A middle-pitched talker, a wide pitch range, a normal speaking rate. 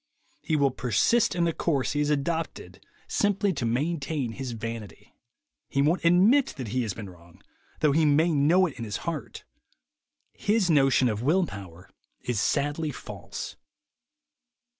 Yes: medium, 145 Hz; wide, 6.3 semitones; average, 155 wpm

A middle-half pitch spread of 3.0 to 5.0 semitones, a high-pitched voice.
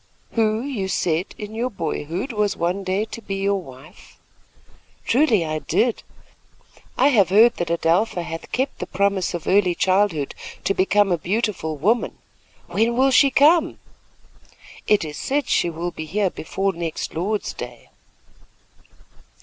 Yes: average, 4.6 semitones; high, 195 Hz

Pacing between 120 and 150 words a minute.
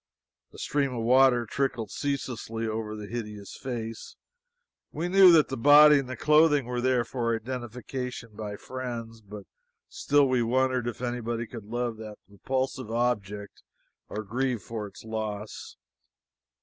Yes: average, 145 wpm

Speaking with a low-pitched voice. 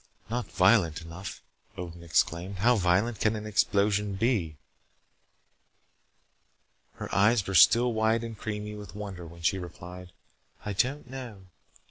Yes: low, 100 Hz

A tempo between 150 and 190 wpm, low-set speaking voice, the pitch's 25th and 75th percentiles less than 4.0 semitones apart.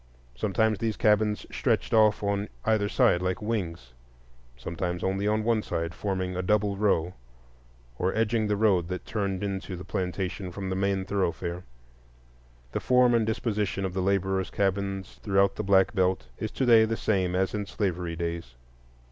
Yes: average, 165 wpm; very low, 95 Hz; narrow, 2.5 semitones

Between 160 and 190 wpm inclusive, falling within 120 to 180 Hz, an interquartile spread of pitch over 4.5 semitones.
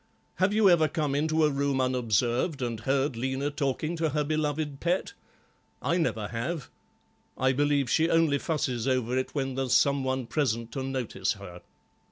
No: average, 170 wpm; low, 135 Hz; average, 3.3 semitones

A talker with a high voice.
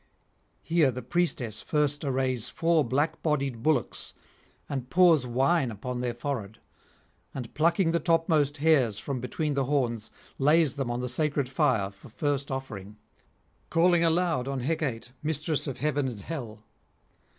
No: medium, 140 Hz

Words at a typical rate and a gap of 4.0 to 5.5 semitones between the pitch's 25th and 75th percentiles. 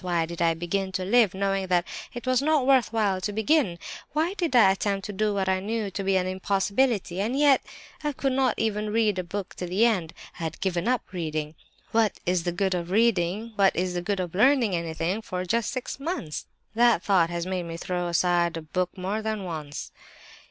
No: fast, 215 wpm; average, 4.3 semitones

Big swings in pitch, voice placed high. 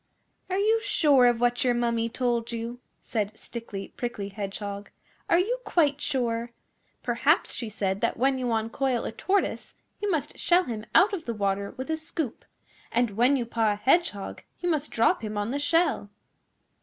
No: average, 4.9 semitones; high, 240 Hz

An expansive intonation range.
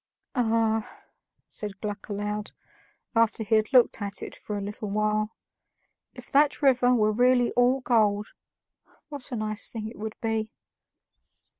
No: narrow, 2.6 semitones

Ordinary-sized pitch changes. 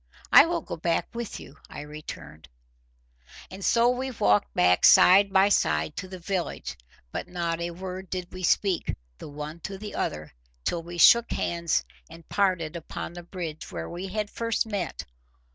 Yes: average, 3.7 semitones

